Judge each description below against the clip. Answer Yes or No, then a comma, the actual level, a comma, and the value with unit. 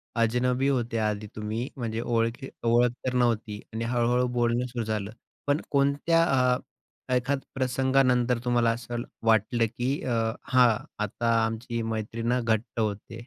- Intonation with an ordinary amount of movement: No, narrow, 1.9 semitones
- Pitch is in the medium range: No, low, 120 Hz